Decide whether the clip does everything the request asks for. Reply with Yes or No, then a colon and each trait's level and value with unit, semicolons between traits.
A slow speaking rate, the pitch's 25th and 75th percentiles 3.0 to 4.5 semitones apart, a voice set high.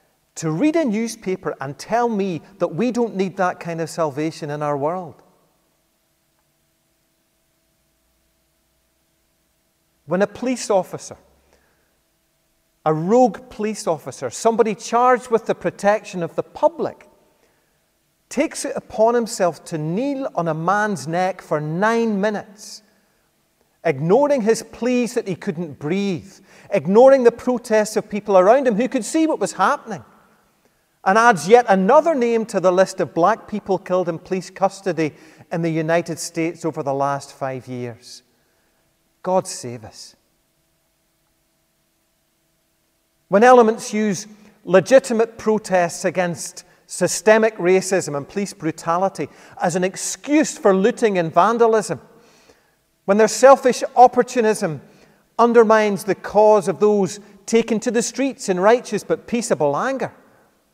No: slow, 130 wpm; average, 5.3 semitones; high, 195 Hz